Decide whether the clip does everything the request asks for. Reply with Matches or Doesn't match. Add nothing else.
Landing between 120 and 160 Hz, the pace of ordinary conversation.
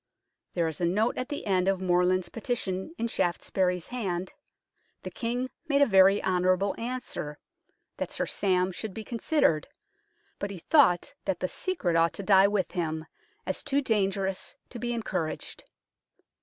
Doesn't match